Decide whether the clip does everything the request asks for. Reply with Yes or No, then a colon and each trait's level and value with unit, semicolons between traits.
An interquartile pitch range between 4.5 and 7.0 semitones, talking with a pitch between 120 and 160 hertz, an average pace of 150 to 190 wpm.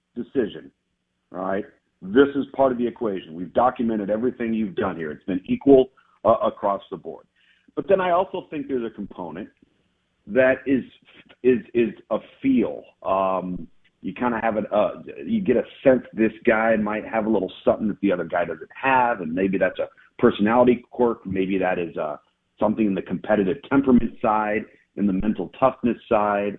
No: average, 4.8 semitones; low, 110 Hz; average, 180 wpm